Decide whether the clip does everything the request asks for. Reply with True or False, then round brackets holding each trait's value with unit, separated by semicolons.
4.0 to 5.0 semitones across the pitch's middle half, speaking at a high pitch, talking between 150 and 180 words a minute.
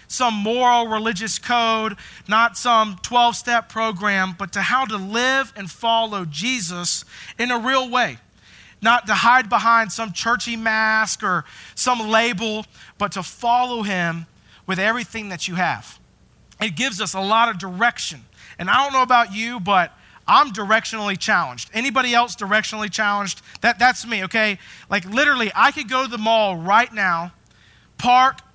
False (3.3 semitones; 225 Hz; 160 wpm)